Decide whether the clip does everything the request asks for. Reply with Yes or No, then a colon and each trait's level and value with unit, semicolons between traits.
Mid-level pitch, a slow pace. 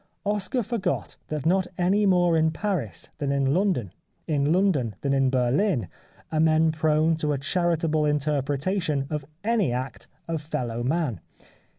No: medium, 155 Hz; average, 150 wpm